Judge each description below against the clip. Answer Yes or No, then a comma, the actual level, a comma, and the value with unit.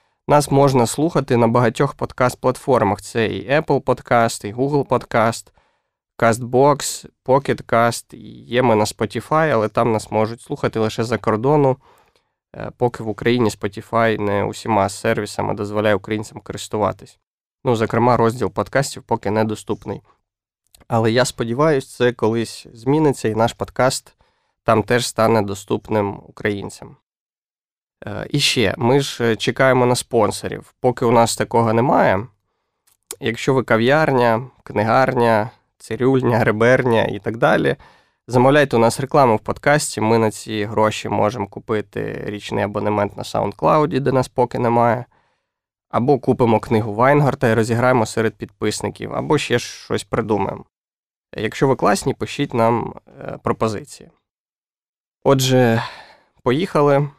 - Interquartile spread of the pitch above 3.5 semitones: No, average, 3.2 semitones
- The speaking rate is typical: Yes, average, 125 wpm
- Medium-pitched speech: No, low, 115 Hz